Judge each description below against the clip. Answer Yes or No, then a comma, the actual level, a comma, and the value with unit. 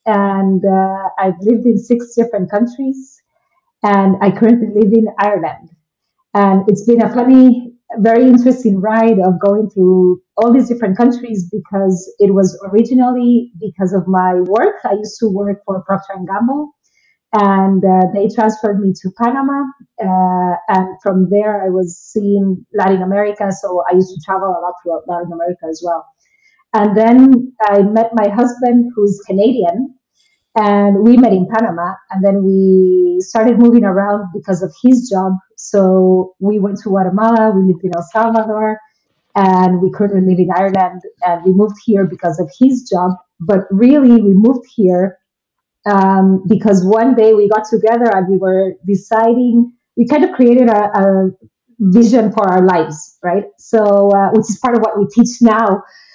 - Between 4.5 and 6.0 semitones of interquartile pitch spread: No, average, 3.4 semitones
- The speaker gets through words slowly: No, average, 170 wpm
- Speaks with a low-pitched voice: No, high, 205 Hz